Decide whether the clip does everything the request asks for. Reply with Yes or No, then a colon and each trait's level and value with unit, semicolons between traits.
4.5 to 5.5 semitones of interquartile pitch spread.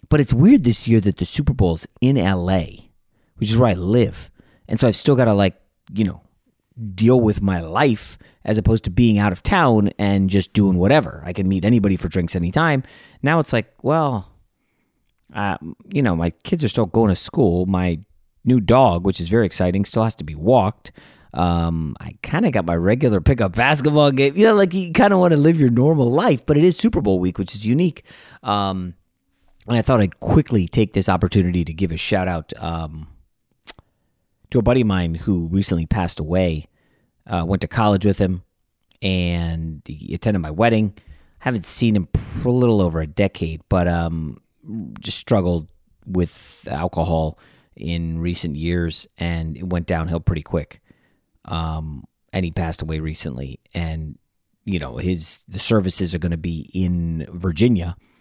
Yes: average, 4.9 semitones